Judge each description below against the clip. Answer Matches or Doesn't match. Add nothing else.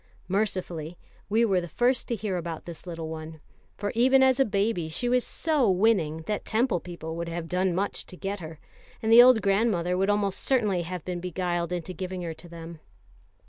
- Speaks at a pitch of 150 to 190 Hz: Matches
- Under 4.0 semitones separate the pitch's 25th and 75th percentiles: Doesn't match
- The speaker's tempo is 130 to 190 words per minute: Doesn't match